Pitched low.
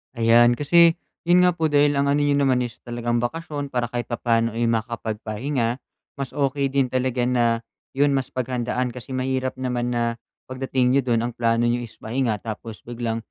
Yes: low, 125 Hz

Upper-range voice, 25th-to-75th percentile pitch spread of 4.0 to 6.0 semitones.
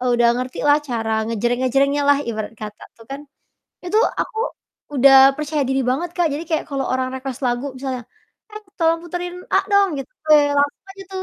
Yes: very high, 275 Hz; average, 4.3 semitones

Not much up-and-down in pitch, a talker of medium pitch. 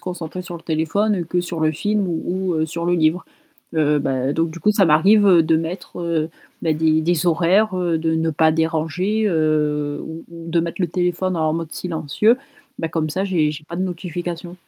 Yes: narrow, 2.2 semitones; medium, 165 Hz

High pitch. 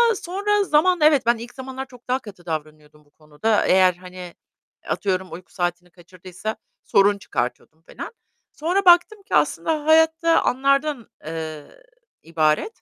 Yes: high, 210 Hz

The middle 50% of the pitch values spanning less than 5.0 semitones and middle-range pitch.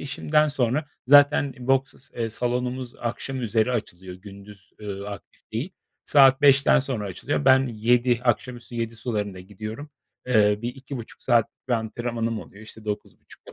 No: average, 3.7 semitones; low, 120 Hz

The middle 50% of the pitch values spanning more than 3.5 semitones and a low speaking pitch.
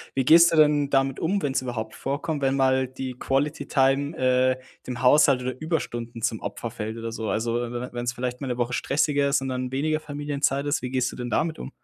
No: average, 2.7 semitones; low, 130 Hz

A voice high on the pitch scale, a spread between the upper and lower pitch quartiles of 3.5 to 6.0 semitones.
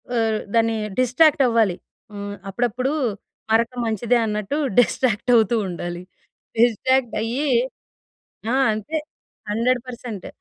No: high, 230 Hz; average, 2.8 semitones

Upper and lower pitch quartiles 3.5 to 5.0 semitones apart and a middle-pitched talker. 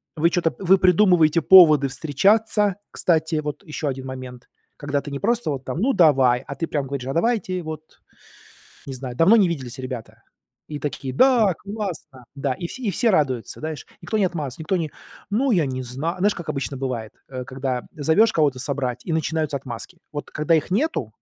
No: wide, 5.5 semitones; medium, 155 Hz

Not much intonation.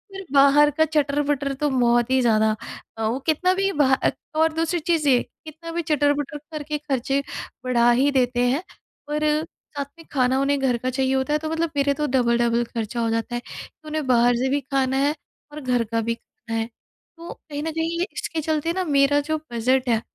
No: average, 3.7 semitones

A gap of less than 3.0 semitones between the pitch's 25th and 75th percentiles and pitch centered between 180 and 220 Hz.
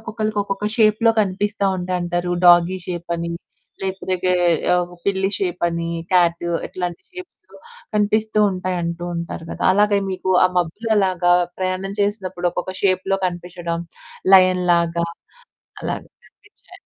Yes: narrow, 2.4 semitones; medium, 185 Hz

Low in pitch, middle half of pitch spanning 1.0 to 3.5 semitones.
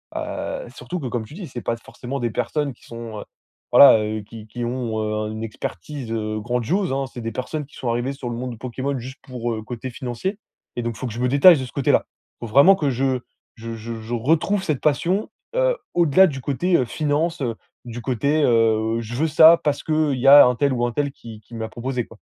No: low, 125 Hz; average, 4.0 semitones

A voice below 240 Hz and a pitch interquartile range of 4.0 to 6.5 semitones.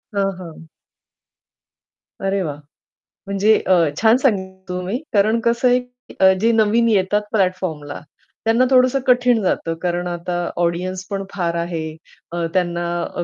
Yes: high, 190 Hz; average, 4.5 semitones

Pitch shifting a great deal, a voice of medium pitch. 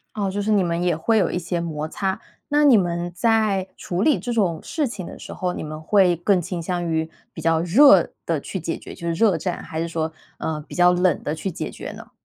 No: average, 3.3 semitones; medium, 175 Hz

